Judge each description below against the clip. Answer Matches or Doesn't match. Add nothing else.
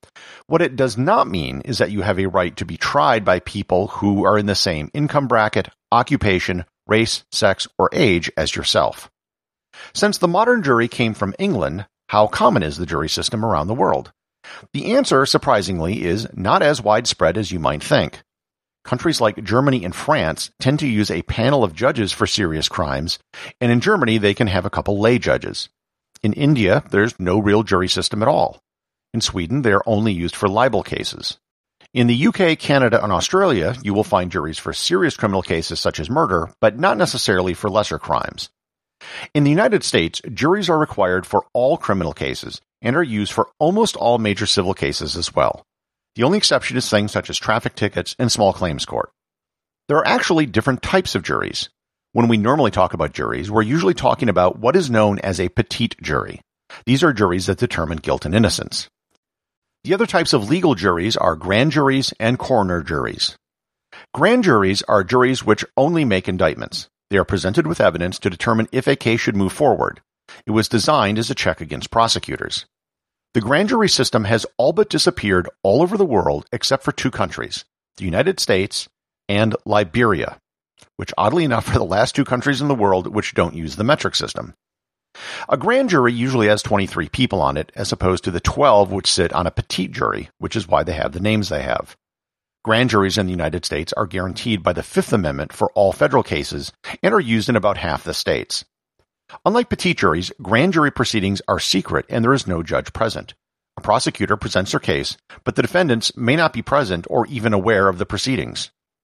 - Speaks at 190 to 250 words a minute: Matches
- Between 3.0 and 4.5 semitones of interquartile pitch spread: Doesn't match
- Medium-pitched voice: Doesn't match